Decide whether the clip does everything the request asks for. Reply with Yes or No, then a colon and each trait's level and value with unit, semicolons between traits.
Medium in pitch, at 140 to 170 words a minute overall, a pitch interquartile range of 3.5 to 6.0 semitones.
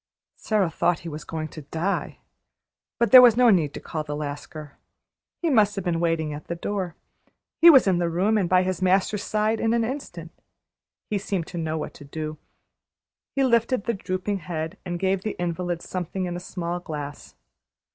No: medium, 180 Hz; average, 195 wpm; average, 4.3 semitones